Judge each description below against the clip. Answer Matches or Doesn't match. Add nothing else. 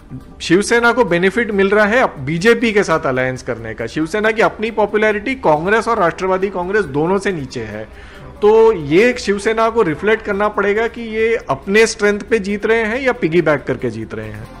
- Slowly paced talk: Doesn't match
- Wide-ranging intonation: Matches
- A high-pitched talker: Matches